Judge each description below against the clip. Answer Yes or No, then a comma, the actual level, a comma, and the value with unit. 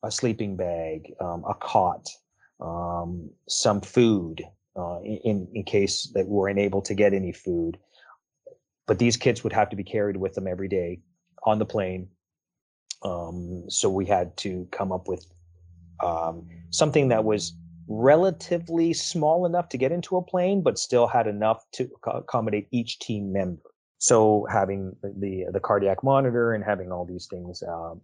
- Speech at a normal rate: Yes, average, 165 wpm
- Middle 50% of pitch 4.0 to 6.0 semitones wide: Yes, average, 4.8 semitones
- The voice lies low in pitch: Yes, low, 100 Hz